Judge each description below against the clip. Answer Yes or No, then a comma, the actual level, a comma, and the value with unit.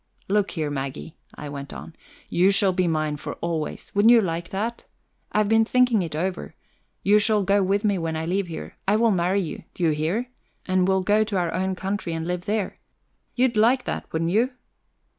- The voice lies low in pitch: No, high, 190 Hz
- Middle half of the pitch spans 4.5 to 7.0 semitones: No, average, 4.1 semitones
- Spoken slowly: No, fast, 205 wpm